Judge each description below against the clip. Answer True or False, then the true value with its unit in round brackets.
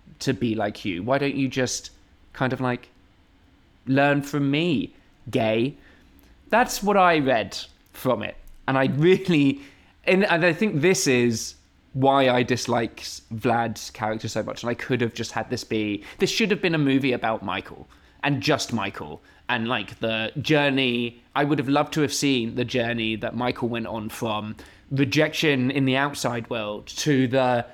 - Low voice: True (125 Hz)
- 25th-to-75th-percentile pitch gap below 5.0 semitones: True (4.1 semitones)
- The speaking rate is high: False (175 wpm)